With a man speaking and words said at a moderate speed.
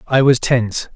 Yes: male; average, 190 wpm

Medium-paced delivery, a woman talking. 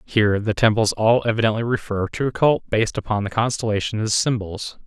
No: average, 185 wpm; male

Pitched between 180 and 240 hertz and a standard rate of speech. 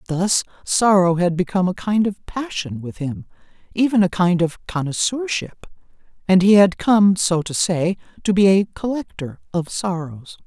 Yes: medium, 185 Hz; average, 160 wpm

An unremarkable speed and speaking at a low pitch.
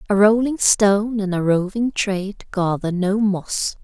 No: average, 155 wpm; high, 200 Hz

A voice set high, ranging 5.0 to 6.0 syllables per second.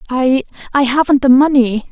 Yes: very high, 265 Hz; 5.1 syllables/s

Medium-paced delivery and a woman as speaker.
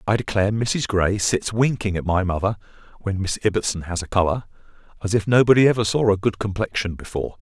No: average, 195 wpm; male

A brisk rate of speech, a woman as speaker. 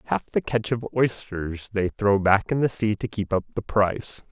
No: fast, 220 wpm; male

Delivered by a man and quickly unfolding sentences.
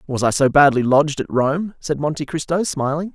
Yes: male; fast, 210 wpm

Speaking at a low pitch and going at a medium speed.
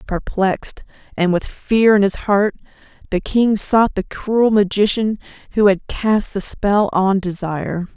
No: high, 200 Hz; average, 150 wpm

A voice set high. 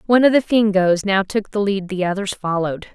Yes: high, 200 Hz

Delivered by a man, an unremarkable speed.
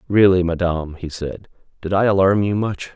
Yes: male; average, 185 wpm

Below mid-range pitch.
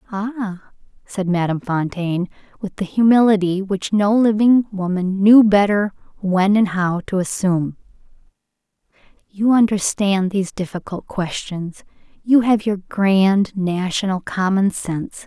No: high, 195 Hz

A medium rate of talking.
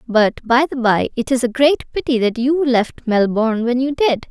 No: fast, 225 wpm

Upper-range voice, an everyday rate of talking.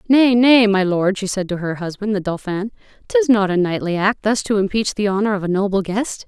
No: high, 200 Hz; fast, 250 wpm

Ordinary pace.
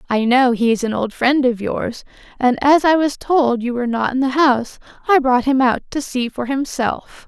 No: fast, 225 wpm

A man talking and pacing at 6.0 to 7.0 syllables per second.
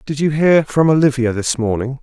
No: male; 5.2 syllables/s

